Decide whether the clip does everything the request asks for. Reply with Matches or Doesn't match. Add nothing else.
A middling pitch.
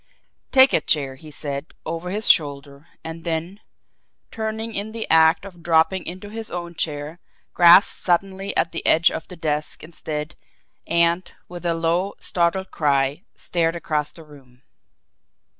Matches